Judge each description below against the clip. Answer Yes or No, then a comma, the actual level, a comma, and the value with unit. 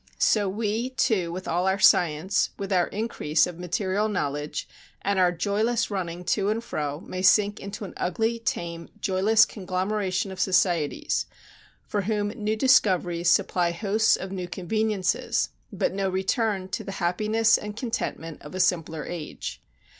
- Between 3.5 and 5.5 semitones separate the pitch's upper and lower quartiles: No, average, 3.1 semitones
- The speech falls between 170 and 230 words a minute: No, average, 155 wpm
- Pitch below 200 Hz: Yes, high, 190 Hz